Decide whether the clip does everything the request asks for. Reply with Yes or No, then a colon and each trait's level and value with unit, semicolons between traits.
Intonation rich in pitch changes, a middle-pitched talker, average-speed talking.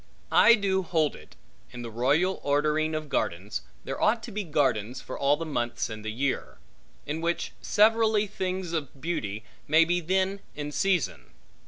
Yes: wide, 6.4 semitones; medium, 155 Hz; average, 170 wpm